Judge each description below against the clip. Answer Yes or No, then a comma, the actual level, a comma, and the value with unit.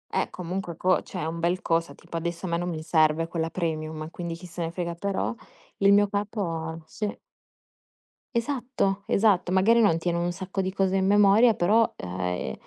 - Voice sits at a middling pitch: Yes, medium, 175 Hz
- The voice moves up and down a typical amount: Yes, average, 3.1 semitones